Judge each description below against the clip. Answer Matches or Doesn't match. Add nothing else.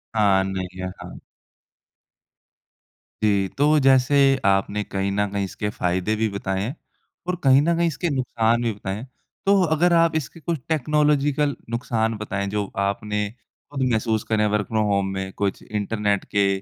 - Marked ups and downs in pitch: Matches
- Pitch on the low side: Matches